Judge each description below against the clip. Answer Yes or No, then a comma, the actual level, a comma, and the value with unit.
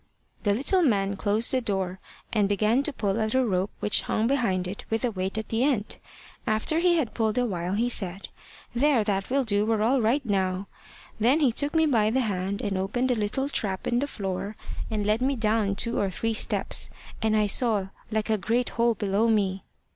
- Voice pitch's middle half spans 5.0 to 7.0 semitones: No, average, 3.5 semitones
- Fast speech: Yes, fast, 215 wpm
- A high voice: Yes, high, 220 Hz